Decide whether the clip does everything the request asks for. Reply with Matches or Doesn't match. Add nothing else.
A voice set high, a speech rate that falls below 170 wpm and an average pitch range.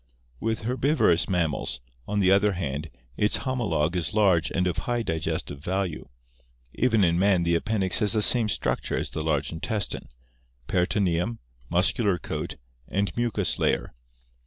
Doesn't match